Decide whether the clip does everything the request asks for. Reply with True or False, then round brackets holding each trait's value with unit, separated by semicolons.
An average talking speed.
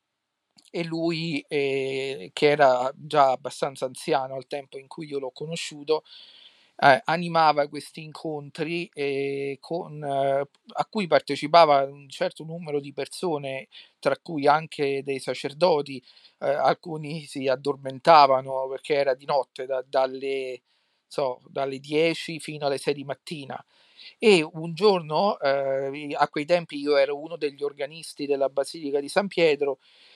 True (140 wpm)